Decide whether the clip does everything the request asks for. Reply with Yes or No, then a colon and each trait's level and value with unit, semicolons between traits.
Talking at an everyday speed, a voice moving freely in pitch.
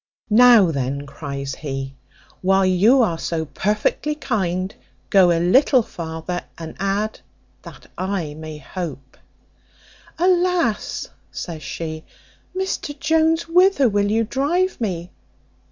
No: slow, 115 wpm; wide, 8.5 semitones